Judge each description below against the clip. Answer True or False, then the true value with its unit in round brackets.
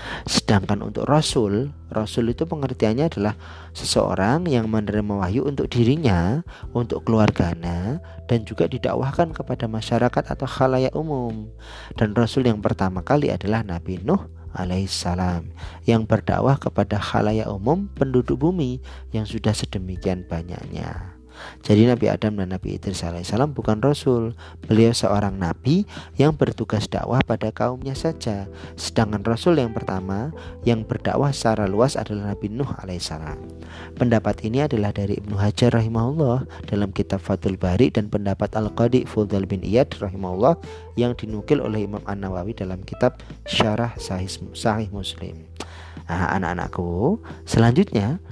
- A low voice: True (105 Hz)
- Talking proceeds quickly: False (130 wpm)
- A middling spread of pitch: True (4.5 semitones)